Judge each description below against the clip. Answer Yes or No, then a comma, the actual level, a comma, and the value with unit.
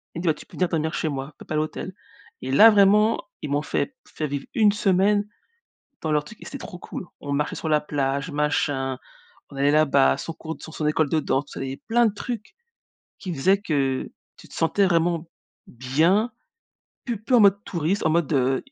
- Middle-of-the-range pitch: Yes, medium, 160 Hz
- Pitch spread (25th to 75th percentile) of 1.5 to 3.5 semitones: No, wide, 5.6 semitones